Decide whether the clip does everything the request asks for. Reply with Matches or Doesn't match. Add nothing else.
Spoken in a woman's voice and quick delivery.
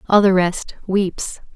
Doesn't match